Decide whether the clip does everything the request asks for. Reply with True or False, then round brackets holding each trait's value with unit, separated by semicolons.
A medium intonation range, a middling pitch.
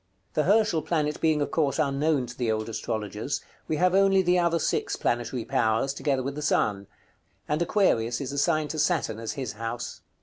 False (5.7 semitones; 145 Hz)